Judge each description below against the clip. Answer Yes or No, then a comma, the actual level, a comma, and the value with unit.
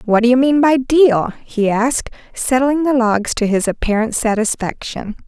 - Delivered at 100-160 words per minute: No, average, 170 wpm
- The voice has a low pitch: No, high, 240 Hz